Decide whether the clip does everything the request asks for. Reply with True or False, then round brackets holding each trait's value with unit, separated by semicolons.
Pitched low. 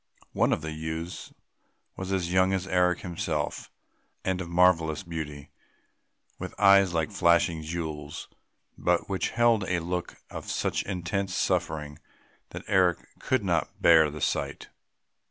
True (85 Hz)